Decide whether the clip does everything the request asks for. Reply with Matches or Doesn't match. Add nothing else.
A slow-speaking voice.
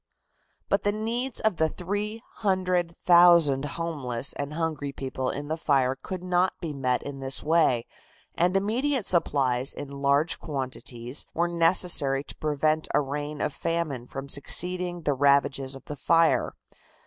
Doesn't match